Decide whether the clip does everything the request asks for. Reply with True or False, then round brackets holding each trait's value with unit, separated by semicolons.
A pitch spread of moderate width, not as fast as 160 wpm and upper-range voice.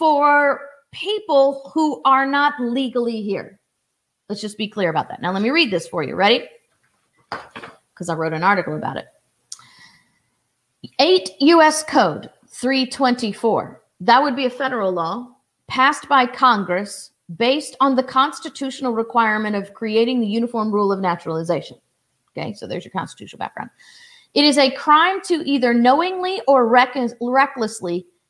True (4.7 semitones; 145 wpm; 255 Hz)